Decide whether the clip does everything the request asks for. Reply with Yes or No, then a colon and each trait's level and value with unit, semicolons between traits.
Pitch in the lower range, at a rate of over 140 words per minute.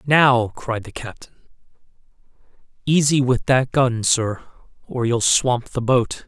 No: low, 125 Hz; slow, 135 wpm